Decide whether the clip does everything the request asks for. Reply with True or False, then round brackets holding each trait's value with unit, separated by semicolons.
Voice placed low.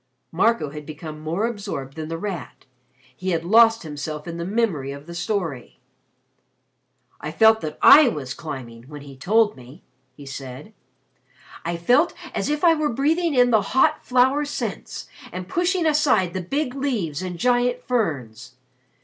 False (185 Hz)